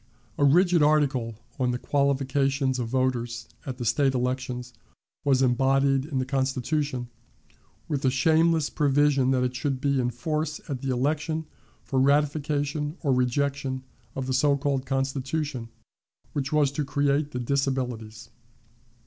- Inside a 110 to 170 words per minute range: Yes, average, 140 wpm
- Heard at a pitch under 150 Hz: Yes, low, 135 Hz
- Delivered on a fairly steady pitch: Yes, narrow, 2.2 semitones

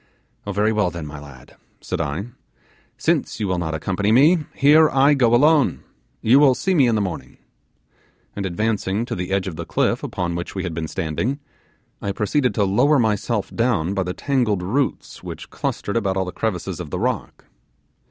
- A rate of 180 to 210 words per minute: Yes, average, 190 wpm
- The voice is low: Yes, low, 105 Hz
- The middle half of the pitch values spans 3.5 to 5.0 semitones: No, wide, 5.6 semitones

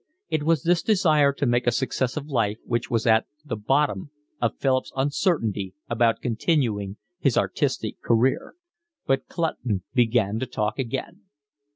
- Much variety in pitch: No, average, 4.5 semitones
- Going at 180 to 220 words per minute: No, average, 150 wpm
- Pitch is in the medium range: No, low, 125 Hz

